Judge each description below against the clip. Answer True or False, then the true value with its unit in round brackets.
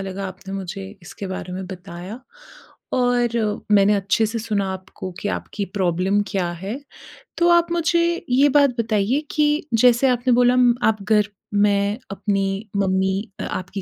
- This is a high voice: True (205 Hz)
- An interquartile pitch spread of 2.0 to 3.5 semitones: False (4.1 semitones)